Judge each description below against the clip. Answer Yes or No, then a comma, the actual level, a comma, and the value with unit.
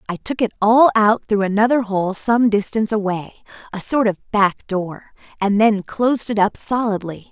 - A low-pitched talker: No, high, 210 Hz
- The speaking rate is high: No, average, 180 wpm